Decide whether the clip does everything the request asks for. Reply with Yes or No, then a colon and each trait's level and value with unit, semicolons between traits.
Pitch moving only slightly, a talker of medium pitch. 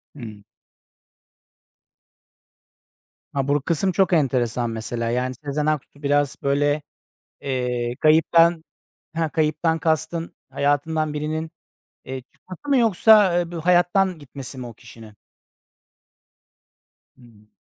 No: average, 4.5 semitones; medium, 150 Hz